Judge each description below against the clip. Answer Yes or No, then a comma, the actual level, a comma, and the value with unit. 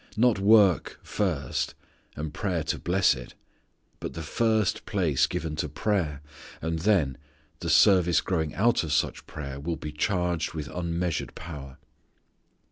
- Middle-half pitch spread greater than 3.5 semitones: Yes, average, 4.2 semitones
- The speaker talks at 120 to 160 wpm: Yes, average, 140 wpm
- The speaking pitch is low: Yes, very low, 85 Hz